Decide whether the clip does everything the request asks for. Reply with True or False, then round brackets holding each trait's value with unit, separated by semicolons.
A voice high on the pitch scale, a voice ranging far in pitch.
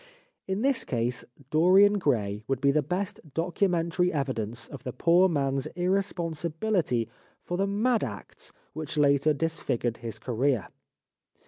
False (155 Hz; 5.9 semitones)